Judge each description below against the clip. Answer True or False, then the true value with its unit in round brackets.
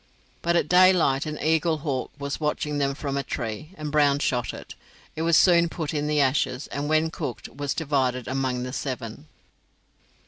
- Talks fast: False (175 wpm)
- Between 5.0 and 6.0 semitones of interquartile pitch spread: False (2.8 semitones)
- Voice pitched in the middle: True (145 Hz)